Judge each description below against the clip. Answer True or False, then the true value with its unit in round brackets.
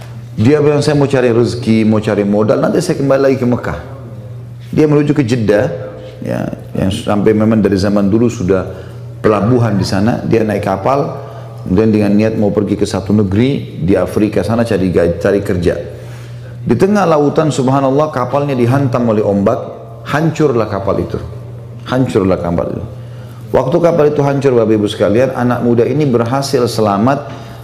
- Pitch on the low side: True (120 Hz)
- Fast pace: True (160 wpm)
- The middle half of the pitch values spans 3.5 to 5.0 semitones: True (3.9 semitones)